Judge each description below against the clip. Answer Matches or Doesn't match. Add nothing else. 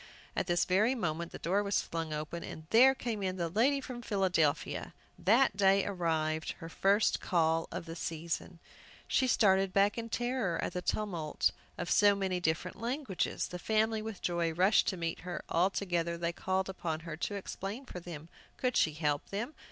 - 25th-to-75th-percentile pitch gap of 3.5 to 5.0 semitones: Matches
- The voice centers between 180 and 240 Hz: Matches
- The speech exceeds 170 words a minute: Matches